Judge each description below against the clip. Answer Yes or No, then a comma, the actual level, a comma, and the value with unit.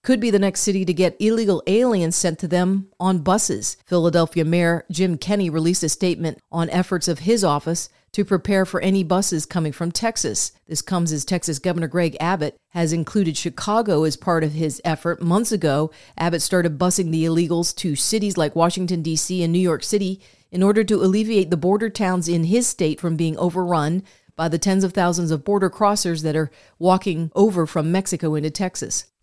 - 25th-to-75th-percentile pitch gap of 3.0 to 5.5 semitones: No, narrow, 2.6 semitones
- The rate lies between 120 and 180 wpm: No, average, 195 wpm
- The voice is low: No, medium, 175 Hz